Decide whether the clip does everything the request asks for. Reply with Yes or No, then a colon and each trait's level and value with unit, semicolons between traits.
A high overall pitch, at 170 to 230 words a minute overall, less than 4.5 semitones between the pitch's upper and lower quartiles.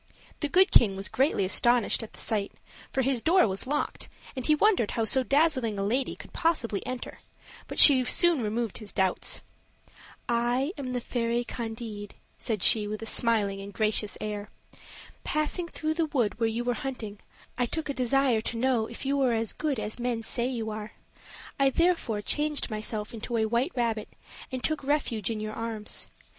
Yes: high, 235 Hz; average, 185 wpm; average, 3.9 semitones